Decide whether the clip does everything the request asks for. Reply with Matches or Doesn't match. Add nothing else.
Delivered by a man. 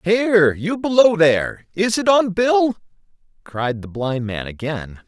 Matches